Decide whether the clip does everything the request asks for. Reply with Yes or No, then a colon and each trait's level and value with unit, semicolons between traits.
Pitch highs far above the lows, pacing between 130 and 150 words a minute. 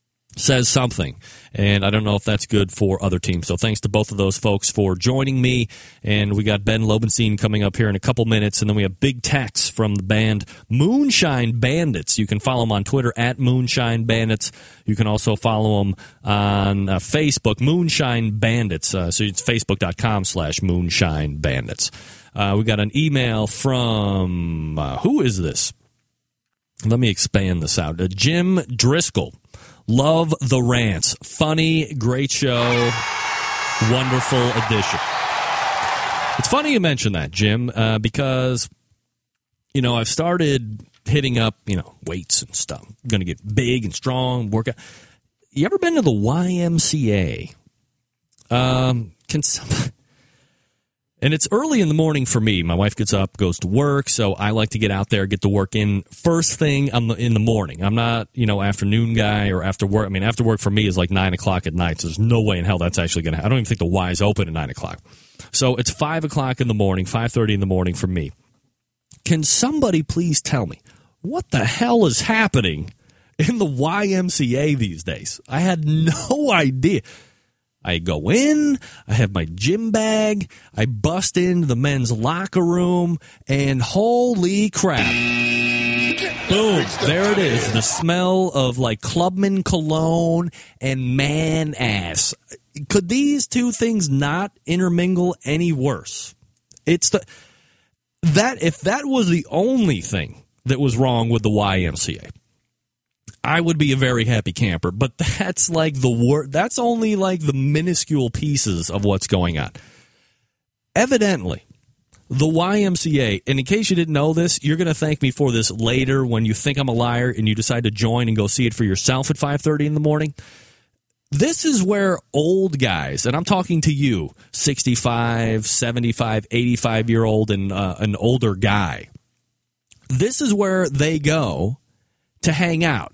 No: wide, 6.4 semitones; average, 170 wpm